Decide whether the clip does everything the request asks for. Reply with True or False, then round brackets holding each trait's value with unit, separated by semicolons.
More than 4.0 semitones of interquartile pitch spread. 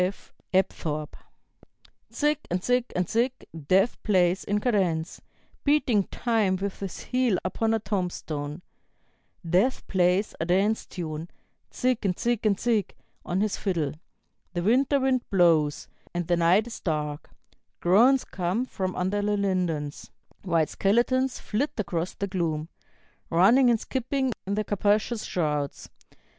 True (4.8 semitones)